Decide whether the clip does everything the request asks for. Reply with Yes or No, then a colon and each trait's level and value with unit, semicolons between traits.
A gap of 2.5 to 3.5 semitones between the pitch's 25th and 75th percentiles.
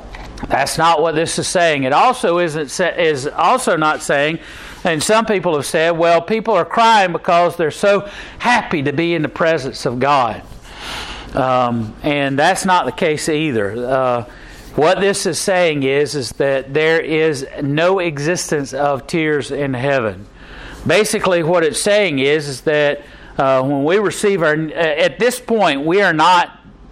No: average, 4.4 semitones